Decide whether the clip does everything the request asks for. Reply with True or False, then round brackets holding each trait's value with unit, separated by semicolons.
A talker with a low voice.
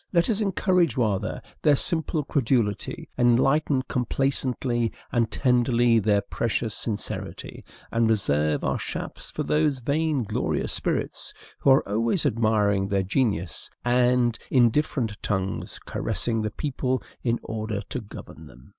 True (120 Hz)